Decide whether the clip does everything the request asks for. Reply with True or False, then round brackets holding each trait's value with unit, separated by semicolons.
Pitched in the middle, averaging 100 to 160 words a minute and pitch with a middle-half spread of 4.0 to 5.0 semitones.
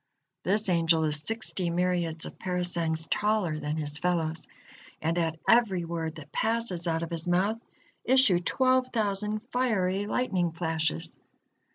True (175 Hz; 140 wpm; 4.5 semitones)